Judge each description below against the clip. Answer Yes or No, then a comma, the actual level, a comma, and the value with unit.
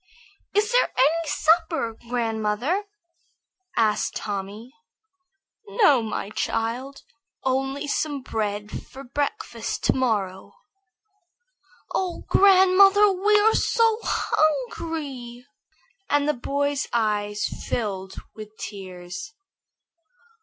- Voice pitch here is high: Yes, very high, 265 Hz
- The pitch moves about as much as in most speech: No, wide, 7.5 semitones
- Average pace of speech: No, slow, 90 wpm